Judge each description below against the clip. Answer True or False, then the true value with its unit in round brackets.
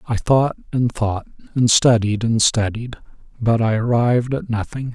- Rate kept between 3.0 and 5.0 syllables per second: True (4.5 syllables/s)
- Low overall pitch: True (115 Hz)